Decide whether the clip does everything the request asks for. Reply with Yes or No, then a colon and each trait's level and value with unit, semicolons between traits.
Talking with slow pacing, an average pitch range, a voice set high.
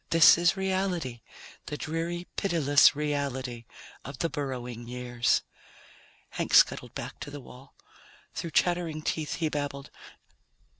No: slow, 120 wpm; average, 4.3 semitones; medium, 145 Hz